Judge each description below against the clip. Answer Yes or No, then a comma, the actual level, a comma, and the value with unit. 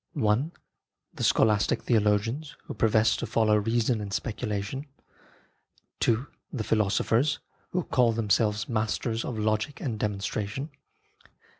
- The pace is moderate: No, slow, 115 wpm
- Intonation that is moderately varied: No, narrow, 2.3 semitones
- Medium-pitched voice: No, low, 110 Hz